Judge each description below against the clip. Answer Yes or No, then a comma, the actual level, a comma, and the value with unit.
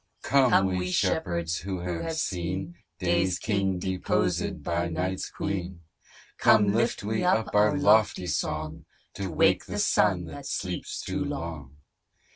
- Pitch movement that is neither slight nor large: Yes, average, 3.2 semitones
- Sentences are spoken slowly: Yes, slow, 130 wpm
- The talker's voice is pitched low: Yes, very low, 95 Hz